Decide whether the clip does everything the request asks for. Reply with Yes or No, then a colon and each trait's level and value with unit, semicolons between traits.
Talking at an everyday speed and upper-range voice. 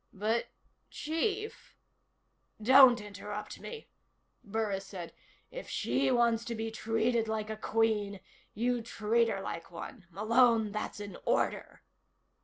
No: slow, 125 wpm; high, 220 Hz